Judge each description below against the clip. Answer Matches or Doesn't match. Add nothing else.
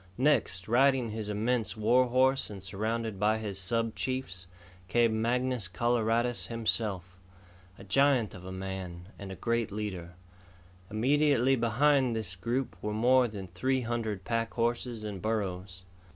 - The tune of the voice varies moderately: Matches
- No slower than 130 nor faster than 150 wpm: Matches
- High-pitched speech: Doesn't match